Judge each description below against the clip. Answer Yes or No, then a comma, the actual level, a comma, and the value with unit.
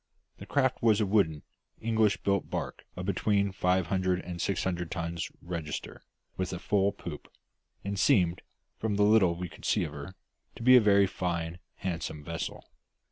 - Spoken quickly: No, average, 175 wpm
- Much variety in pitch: No, average, 3.0 semitones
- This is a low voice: Yes, very low, 95 Hz